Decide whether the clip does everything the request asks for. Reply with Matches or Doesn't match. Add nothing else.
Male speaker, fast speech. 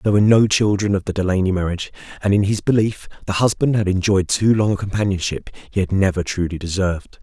Matches